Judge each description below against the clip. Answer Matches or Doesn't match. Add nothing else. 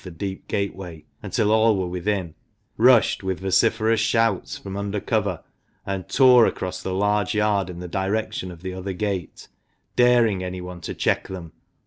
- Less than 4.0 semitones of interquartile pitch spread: Matches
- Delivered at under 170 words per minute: Matches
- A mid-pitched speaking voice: Doesn't match